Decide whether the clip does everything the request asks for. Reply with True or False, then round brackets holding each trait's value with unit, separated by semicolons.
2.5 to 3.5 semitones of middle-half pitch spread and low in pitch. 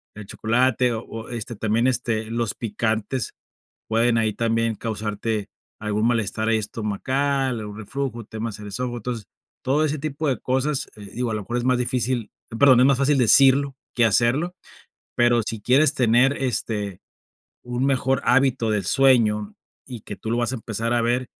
True (2.9 semitones; 120 Hz)